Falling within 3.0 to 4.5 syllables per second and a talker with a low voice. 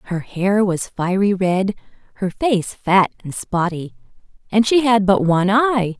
No: 4.3 syllables/s; high, 195 Hz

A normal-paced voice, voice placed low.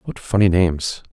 Yes: average, 155 wpm; very low, 95 Hz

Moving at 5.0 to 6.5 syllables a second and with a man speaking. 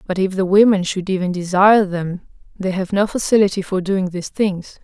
No: 5.4 syllables/s; female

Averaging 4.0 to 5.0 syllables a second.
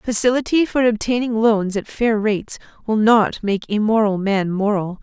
Yes: 4.7 syllables/s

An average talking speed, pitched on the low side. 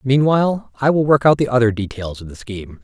No: fast, 230 wpm; low, 125 Hz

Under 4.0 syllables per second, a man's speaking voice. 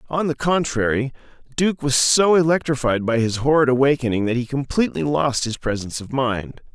No: 5.5 syllables/s; male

